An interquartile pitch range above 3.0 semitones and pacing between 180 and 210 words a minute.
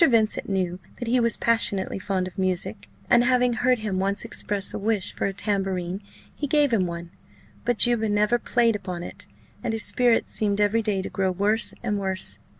Yes: average, 3.5 semitones; average, 195 wpm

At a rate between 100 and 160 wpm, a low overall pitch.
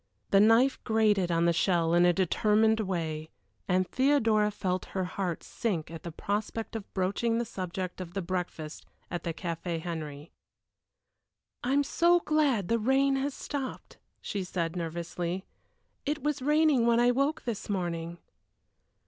No: average, 155 wpm; high, 195 Hz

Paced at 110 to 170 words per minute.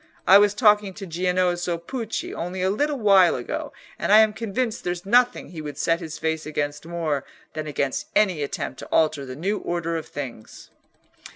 No: average, 185 wpm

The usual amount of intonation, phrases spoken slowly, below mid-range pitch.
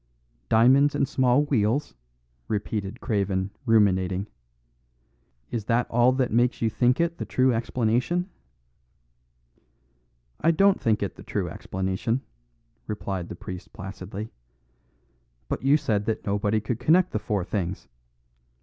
Yes: average, 4.2 semitones; slow, 125 wpm; low, 110 Hz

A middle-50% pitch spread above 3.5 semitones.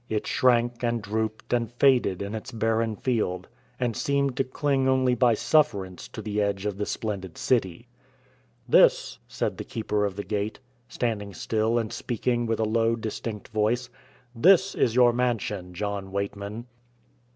No: average, 2.9 semitones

